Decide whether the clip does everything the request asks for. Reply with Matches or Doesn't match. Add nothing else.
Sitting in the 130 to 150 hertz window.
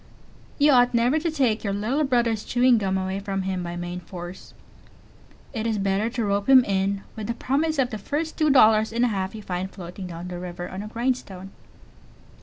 Doesn't match